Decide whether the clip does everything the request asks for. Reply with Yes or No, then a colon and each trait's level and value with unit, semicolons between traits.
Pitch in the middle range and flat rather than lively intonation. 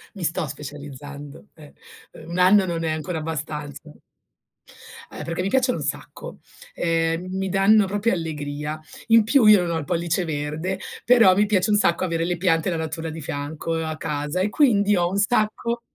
No: medium, 170 Hz; average, 4.0 semitones